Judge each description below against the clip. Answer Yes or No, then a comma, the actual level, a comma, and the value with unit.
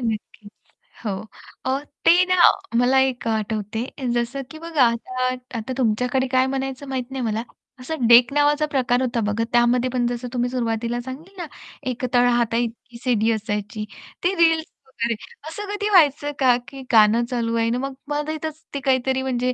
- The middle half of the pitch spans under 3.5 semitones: Yes, average, 2.8 semitones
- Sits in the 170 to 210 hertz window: No, very high, 250 Hz